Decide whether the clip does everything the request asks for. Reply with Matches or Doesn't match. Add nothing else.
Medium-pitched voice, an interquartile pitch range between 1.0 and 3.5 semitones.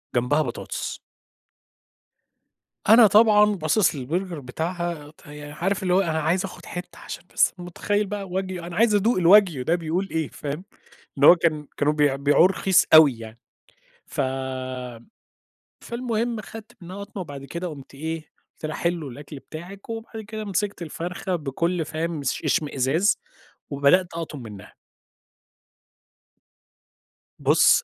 Doesn't match